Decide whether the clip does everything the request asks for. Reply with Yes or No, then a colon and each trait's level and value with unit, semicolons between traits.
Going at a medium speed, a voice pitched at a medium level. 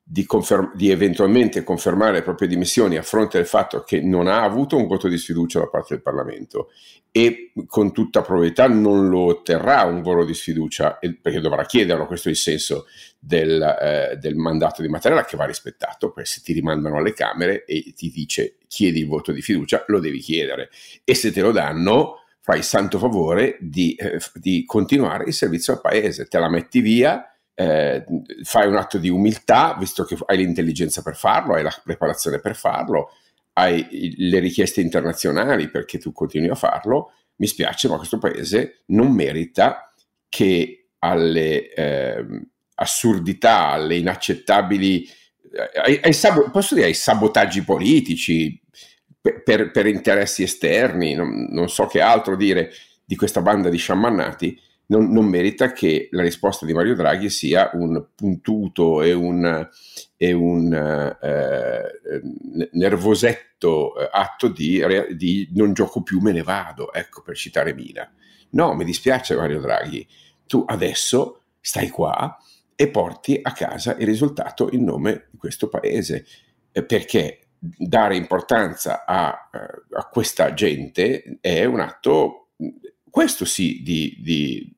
No: average, 155 wpm; very low, 95 Hz